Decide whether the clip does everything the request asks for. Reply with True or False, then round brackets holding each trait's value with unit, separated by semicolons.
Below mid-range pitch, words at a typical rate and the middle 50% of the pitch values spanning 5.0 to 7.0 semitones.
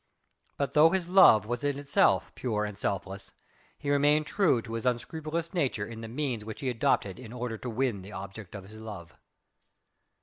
True (120 Hz; 190 wpm; 5.3 semitones)